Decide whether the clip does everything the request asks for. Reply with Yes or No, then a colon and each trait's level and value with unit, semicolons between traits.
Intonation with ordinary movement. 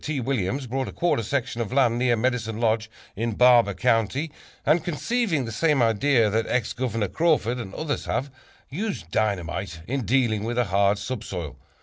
Yes: average, 3.9 semitones